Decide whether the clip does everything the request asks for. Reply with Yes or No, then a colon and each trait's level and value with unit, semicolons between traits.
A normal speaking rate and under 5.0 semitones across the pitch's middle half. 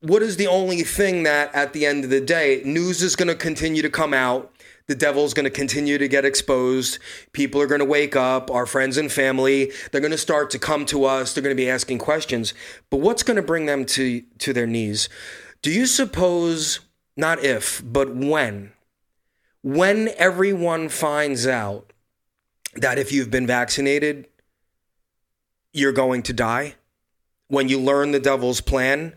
Yes: average, 180 wpm; average, 2.9 semitones